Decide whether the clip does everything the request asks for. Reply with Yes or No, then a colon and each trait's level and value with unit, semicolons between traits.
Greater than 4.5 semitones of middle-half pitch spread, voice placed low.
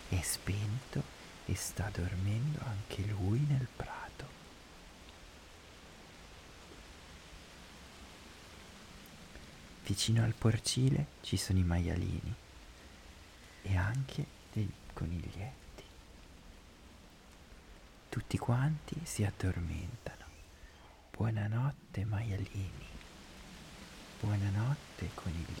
Yes: average, 4.9 semitones; very low, 95 Hz